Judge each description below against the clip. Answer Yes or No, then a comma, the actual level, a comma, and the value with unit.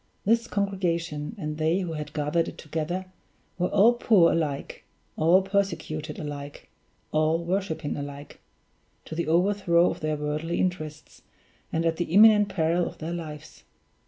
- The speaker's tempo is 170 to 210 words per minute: No, average, 145 wpm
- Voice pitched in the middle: Yes, medium, 165 Hz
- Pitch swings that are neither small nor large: Yes, average, 3.4 semitones